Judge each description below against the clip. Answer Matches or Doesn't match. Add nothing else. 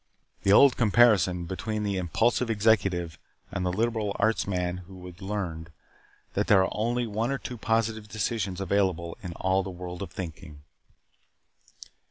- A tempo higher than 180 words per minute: Doesn't match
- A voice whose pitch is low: Matches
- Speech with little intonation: Doesn't match